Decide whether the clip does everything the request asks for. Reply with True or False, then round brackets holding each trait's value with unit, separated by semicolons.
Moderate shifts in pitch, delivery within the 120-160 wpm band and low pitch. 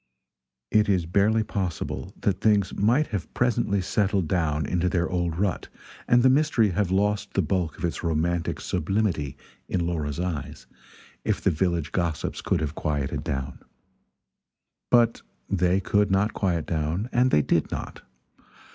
True (4.1 semitones; 150 wpm; 90 Hz)